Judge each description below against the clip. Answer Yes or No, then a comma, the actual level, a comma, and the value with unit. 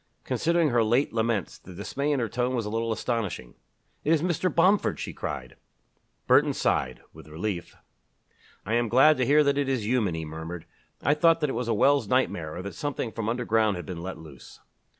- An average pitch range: No, wide, 7.1 semitones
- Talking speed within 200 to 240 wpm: Yes, fast, 205 wpm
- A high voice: No, low, 115 Hz